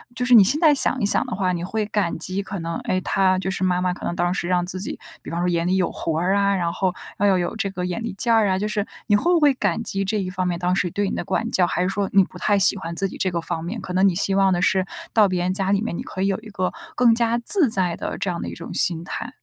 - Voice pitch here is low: No, high, 190 Hz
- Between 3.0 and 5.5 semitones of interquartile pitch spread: No, narrow, 2.5 semitones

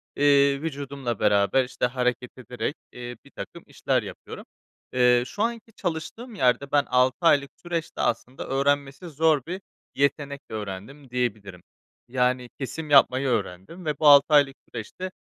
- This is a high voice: No, low, 135 Hz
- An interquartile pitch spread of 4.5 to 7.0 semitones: No, average, 3.2 semitones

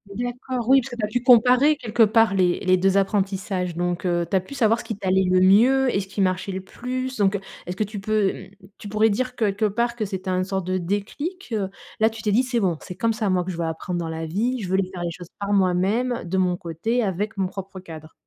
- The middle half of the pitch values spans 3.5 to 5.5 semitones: Yes, average, 3.8 semitones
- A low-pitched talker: No, high, 200 Hz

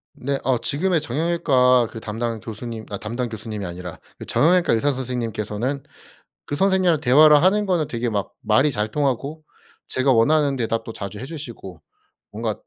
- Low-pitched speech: Yes, low, 125 Hz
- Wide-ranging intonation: No, average, 5.0 semitones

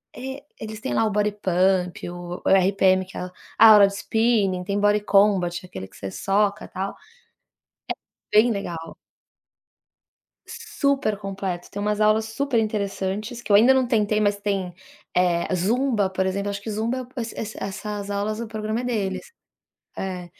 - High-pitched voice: Yes, high, 205 Hz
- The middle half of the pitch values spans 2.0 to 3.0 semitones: Yes, narrow, 2.4 semitones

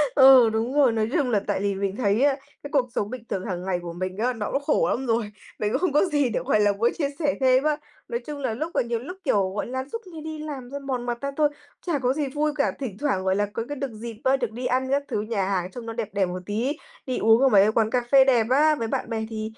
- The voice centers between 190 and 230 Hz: No, high, 245 Hz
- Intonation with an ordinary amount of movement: Yes, average, 4.7 semitones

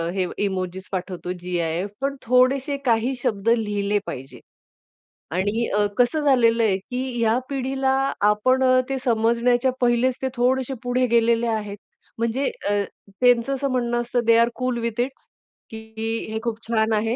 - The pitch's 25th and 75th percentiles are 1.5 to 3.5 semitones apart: Yes, average, 2.8 semitones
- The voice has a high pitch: Yes, high, 235 Hz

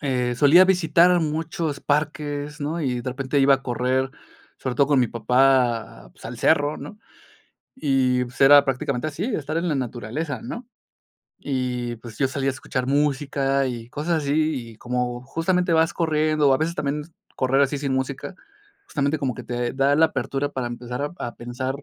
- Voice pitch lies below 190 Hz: Yes, medium, 140 Hz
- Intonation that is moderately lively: Yes, average, 3.2 semitones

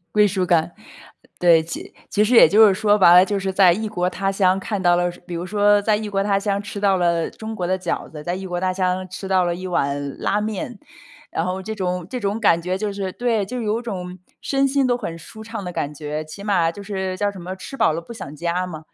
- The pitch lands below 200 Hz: Yes, high, 190 Hz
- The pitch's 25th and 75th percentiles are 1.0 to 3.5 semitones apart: Yes, average, 2.8 semitones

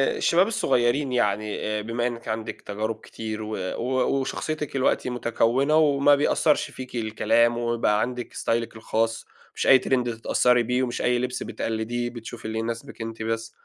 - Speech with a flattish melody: Yes, narrow, 2.1 semitones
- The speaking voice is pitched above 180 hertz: No, low, 120 Hz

